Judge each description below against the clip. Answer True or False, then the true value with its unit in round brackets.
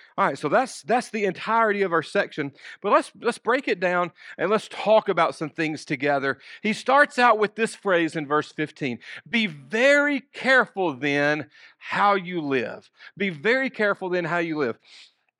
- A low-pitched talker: False (195 Hz)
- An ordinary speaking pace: True (180 wpm)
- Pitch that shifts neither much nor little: False (6.5 semitones)